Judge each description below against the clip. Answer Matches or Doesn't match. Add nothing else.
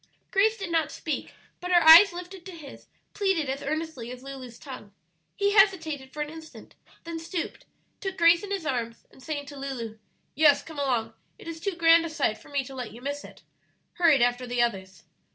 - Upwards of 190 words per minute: Matches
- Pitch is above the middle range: Matches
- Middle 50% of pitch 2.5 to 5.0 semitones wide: Matches